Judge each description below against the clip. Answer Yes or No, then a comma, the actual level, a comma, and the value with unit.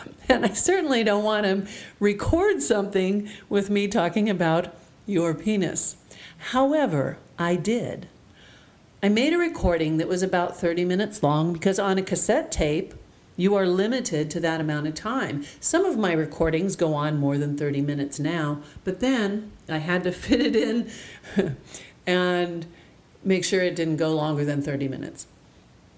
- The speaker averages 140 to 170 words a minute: Yes, average, 160 wpm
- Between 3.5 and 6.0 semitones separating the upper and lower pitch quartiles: Yes, average, 4.5 semitones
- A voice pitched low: No, medium, 180 Hz